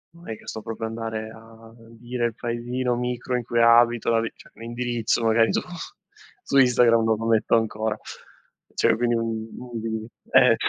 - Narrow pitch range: Yes, narrow, 1.2 semitones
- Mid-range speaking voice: No, low, 115 Hz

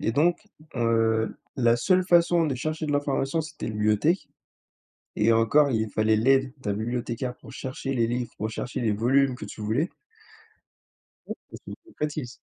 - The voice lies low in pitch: Yes, low, 125 Hz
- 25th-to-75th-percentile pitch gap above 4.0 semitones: Yes, average, 4.5 semitones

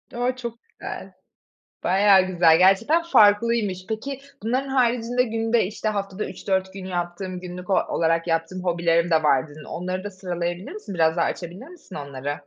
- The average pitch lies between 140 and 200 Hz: Yes, medium, 185 Hz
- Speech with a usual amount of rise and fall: Yes, average, 4.6 semitones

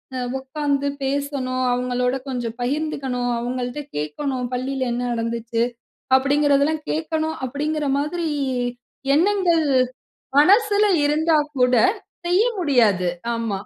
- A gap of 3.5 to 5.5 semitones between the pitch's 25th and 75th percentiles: Yes, average, 3.8 semitones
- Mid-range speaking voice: No, very high, 275 Hz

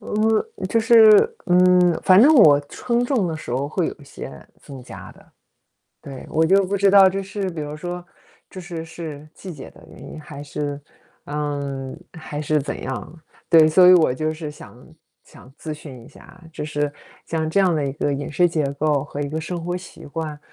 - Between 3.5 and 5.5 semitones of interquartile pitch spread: Yes, average, 3.9 semitones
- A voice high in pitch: No, medium, 160 Hz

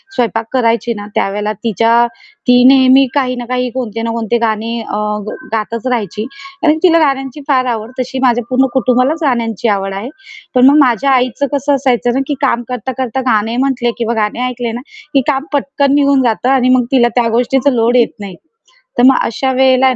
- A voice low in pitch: No, very high, 250 Hz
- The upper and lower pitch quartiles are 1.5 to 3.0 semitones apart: Yes, narrow, 2.5 semitones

